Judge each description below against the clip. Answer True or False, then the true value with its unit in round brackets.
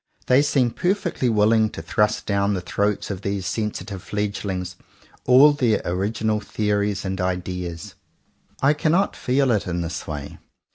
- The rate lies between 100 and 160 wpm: True (150 wpm)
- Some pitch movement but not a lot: True (4.5 semitones)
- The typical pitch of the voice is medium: False (105 Hz)